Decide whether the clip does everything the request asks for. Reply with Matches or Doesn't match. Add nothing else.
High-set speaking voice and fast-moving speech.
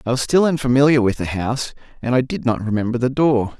Doesn't match